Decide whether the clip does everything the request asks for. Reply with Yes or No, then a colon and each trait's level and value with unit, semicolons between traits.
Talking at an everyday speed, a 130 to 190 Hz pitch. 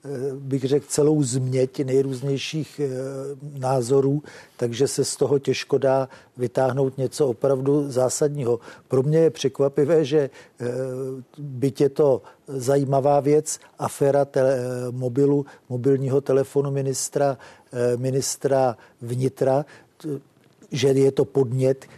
No: slow, 100 wpm; low, 135 Hz